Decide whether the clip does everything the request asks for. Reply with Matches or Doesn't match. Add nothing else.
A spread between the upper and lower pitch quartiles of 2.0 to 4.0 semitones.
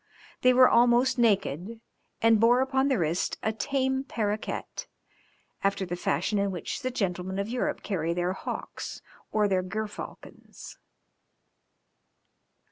Doesn't match